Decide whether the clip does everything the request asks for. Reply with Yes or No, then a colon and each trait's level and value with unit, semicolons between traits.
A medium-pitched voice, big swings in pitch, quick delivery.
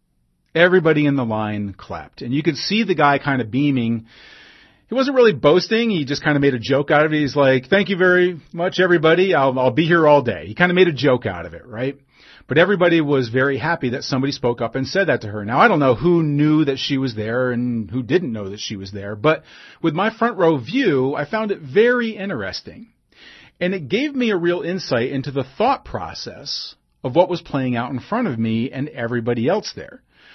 Yes: medium, 145 Hz; wide, 6.0 semitones; fast, 235 wpm